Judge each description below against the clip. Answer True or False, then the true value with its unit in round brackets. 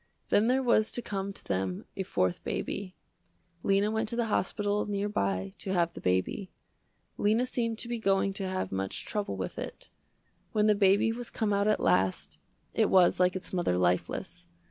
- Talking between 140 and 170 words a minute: False (190 wpm)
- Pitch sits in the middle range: False (195 Hz)